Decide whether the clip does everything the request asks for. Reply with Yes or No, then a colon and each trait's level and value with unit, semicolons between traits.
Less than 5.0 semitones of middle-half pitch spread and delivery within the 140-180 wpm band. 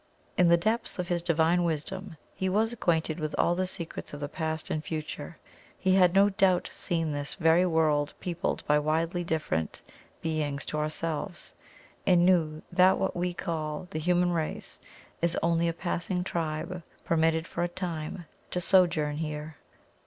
Yes: narrow, 2.4 semitones; average, 165 wpm